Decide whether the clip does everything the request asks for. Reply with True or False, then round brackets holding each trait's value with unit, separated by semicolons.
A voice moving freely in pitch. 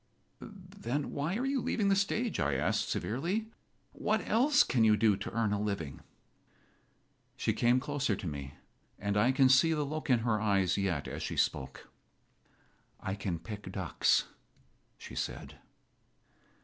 True (8.6 semitones)